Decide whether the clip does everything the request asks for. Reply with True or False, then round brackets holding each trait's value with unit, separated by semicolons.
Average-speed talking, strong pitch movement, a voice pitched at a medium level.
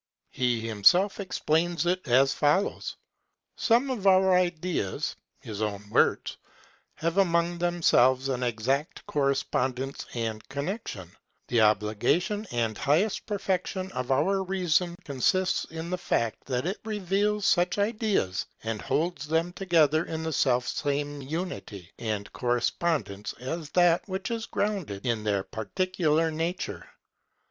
False (125 wpm; 7.1 semitones; 160 Hz)